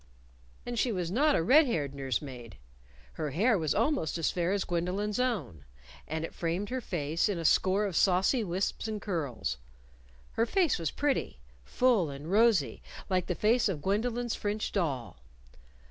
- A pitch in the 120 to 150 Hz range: No, high, 190 Hz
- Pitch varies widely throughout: Yes, wide, 6.2 semitones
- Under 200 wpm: Yes, average, 170 wpm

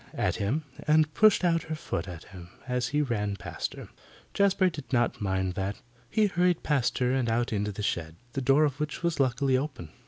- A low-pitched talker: Yes, low, 130 Hz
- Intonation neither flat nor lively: No, wide, 7.0 semitones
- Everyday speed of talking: No, fast, 215 wpm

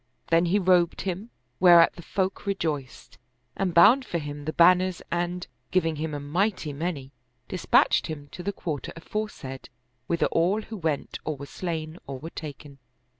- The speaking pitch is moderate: Yes, medium, 170 Hz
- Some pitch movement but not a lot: Yes, average, 3.5 semitones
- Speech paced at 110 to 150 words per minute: No, average, 170 wpm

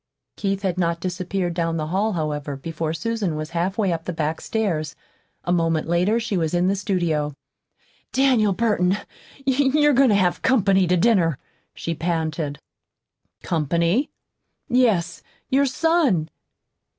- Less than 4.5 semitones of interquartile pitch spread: No, average, 4.9 semitones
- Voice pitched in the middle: Yes, medium, 180 Hz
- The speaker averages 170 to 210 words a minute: No, average, 140 wpm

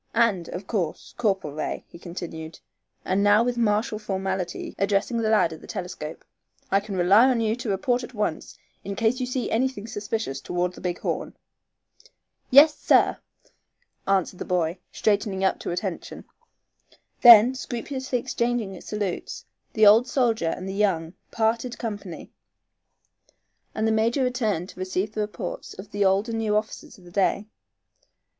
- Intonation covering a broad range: No, average, 3.7 semitones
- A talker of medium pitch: No, high, 210 Hz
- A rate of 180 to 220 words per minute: No, average, 160 wpm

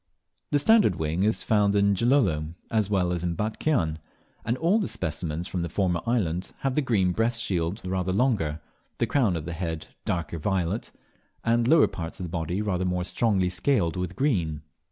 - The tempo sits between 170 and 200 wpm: Yes, average, 190 wpm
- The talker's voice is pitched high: No, very low, 95 Hz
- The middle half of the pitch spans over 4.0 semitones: Yes, average, 5.2 semitones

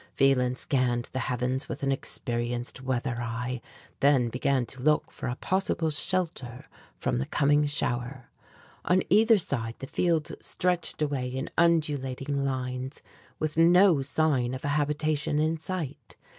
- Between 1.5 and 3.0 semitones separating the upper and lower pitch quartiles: No, average, 3.6 semitones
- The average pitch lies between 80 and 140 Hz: Yes, low, 135 Hz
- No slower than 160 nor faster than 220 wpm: No, average, 145 wpm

